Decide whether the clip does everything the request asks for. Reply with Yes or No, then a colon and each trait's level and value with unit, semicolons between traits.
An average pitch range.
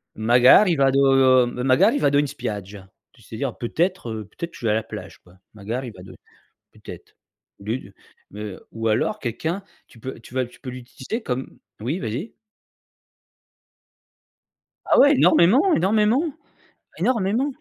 No: wide, 7.6 semitones